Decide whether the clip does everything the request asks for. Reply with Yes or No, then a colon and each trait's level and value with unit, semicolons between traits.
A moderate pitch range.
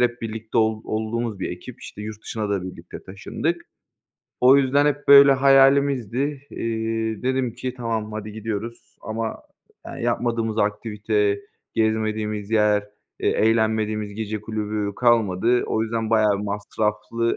No: narrow, 1.8 semitones